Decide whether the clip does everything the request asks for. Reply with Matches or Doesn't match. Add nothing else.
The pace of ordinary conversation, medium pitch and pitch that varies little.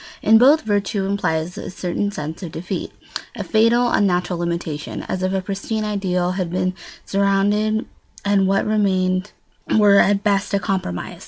Doesn't match